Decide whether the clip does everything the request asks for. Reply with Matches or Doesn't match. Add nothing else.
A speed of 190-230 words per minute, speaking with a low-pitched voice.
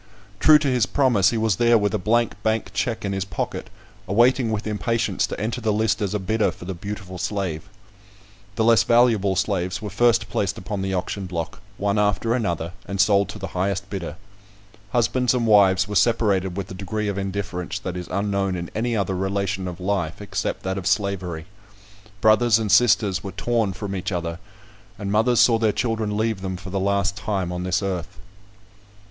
Matches